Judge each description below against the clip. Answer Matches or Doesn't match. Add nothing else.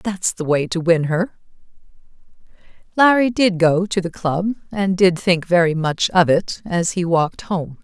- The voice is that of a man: Doesn't match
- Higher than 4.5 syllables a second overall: Doesn't match